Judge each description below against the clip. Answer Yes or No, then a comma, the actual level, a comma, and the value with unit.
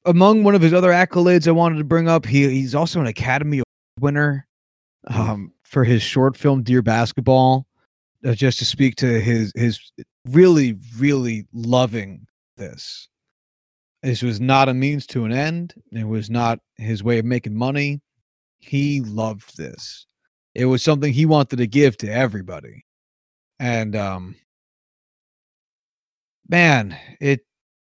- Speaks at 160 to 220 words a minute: No, average, 145 wpm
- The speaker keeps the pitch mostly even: No, average, 4.2 semitones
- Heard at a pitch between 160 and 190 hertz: No, low, 130 Hz